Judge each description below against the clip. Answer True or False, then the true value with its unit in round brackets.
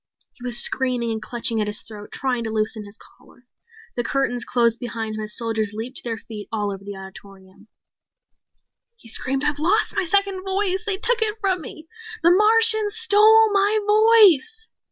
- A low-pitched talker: False (260 Hz)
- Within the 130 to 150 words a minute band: False (180 wpm)